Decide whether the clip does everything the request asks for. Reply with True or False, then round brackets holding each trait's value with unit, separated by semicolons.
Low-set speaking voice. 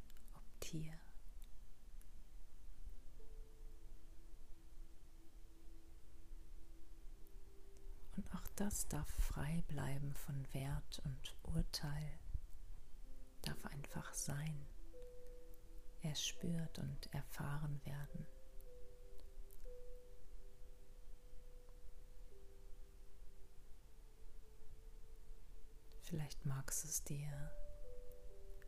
False (145 Hz)